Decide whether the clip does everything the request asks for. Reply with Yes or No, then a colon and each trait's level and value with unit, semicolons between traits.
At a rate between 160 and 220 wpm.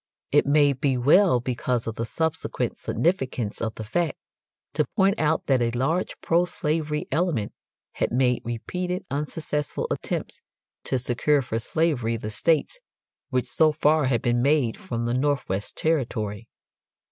No: average, 145 wpm